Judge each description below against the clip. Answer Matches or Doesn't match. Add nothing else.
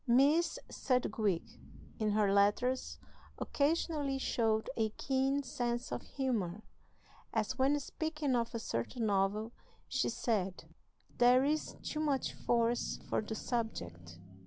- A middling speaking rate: Doesn't match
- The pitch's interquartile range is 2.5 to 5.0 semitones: Matches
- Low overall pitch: Doesn't match